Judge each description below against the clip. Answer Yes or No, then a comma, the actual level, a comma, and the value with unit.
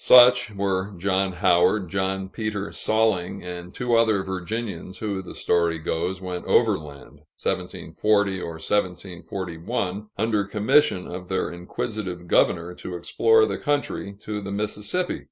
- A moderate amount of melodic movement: Yes, average, 3.1 semitones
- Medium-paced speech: No, slow, 130 wpm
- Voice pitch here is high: No, very low, 95 Hz